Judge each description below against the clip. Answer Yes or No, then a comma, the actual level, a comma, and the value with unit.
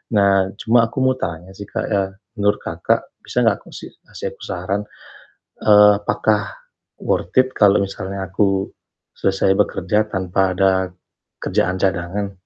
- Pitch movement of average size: No, narrow, 1.6 semitones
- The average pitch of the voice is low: Yes, very low, 95 Hz